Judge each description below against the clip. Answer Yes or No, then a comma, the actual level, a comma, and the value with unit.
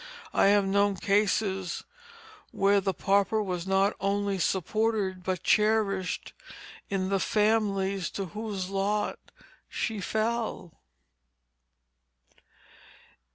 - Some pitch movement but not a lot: No, narrow, 1.6 semitones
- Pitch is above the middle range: Yes, high, 200 Hz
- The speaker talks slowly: Yes, slow, 95 wpm